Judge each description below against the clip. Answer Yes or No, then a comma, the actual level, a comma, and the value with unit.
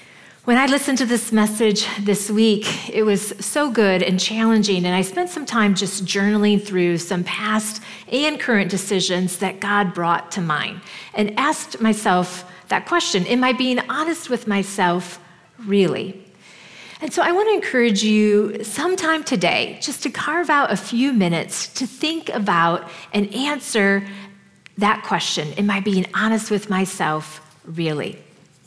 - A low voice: No, high, 205 Hz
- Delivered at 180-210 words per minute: No, average, 155 wpm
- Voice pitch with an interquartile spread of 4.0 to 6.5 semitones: Yes, average, 4.4 semitones